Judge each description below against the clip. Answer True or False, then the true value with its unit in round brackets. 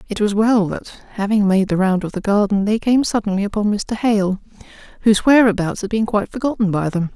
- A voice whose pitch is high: True (205 Hz)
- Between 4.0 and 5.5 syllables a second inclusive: False (5.7 syllables/s)